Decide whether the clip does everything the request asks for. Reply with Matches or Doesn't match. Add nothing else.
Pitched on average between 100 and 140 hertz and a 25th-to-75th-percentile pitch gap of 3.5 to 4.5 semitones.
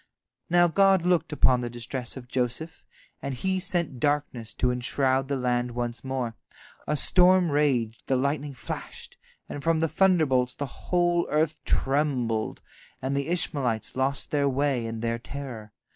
Matches